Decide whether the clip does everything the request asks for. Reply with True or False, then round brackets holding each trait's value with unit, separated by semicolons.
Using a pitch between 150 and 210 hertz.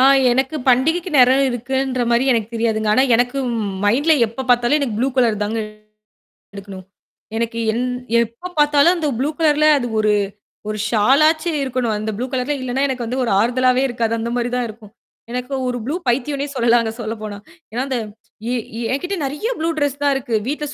False (250 Hz)